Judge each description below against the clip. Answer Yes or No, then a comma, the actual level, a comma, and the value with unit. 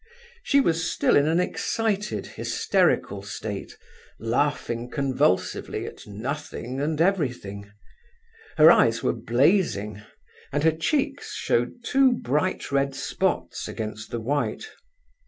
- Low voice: No, medium, 145 Hz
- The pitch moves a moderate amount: No, wide, 7.3 semitones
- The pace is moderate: No, slow, 115 wpm